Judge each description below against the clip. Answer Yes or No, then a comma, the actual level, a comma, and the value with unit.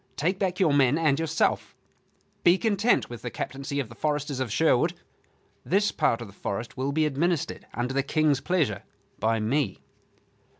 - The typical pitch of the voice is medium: Yes, medium, 145 Hz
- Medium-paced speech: Yes, average, 170 wpm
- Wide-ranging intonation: No, average, 4.8 semitones